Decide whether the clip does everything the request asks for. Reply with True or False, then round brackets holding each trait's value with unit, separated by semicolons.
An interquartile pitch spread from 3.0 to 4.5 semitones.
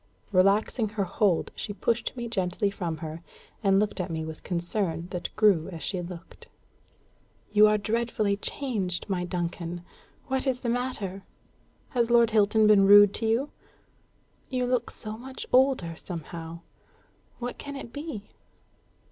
False (4.9 semitones)